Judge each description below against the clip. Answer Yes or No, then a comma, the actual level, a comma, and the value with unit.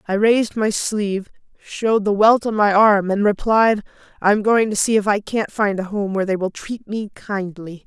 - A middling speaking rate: No, fast, 220 wpm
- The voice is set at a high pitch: Yes, high, 205 Hz